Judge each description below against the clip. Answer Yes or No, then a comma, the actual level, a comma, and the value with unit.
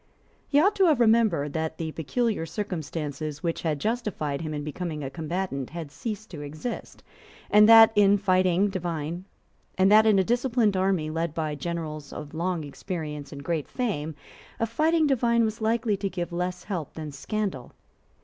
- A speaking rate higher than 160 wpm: No, average, 155 wpm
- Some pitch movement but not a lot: No, wide, 5.9 semitones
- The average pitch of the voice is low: No, medium, 175 Hz